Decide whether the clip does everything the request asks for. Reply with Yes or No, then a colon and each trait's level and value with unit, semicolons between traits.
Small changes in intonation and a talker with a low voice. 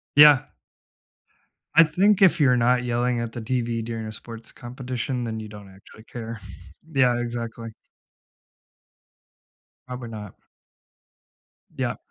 Yes: narrow, 1.8 semitones; low, 120 Hz